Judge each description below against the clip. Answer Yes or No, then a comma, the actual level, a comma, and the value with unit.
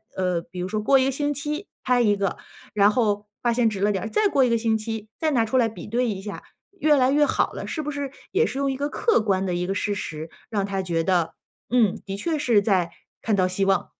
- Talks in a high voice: Yes, high, 220 Hz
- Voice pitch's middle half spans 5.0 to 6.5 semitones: Yes, wide, 5.6 semitones